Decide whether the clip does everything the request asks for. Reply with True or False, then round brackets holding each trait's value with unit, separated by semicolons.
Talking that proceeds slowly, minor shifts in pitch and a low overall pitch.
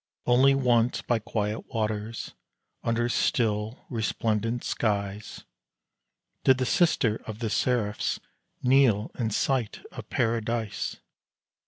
True (105 wpm; 2.3 semitones; 115 Hz)